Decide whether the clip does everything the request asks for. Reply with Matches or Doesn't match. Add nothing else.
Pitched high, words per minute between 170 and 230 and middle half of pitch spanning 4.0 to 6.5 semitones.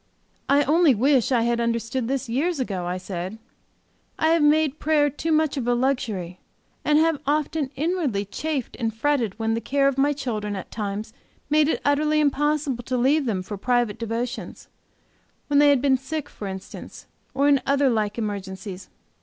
Matches